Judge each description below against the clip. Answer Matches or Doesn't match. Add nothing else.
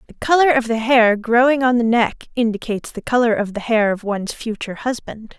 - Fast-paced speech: Matches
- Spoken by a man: Doesn't match